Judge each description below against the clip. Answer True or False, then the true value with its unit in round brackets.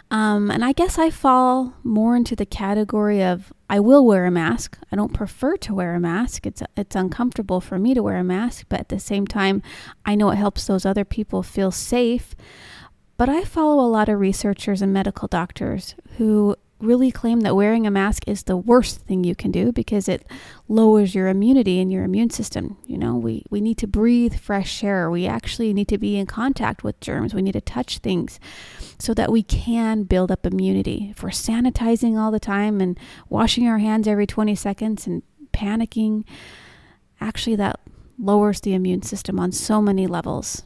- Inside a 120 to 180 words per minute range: False (200 wpm)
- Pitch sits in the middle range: False (210 Hz)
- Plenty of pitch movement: False (3.1 semitones)